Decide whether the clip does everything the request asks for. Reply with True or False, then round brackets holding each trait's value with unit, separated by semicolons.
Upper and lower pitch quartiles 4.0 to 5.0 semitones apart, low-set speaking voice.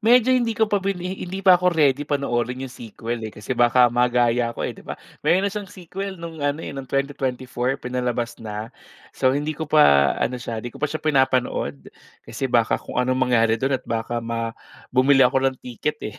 True (4.5 semitones; 130 Hz)